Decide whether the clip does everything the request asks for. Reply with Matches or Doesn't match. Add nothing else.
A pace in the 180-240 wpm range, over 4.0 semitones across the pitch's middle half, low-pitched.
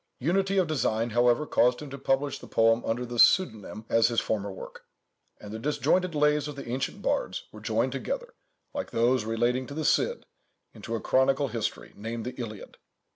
Matches